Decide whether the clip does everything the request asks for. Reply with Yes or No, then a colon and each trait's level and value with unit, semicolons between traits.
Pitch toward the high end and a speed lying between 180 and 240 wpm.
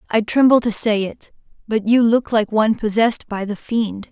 Yes: high, 220 Hz; fast, 205 wpm